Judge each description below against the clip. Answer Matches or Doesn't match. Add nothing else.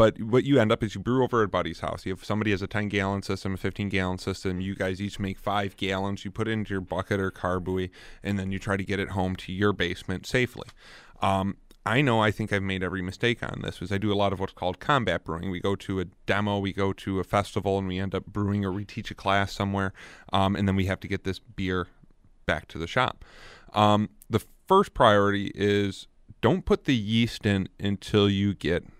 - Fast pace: Matches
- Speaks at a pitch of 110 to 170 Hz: Doesn't match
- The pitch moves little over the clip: Matches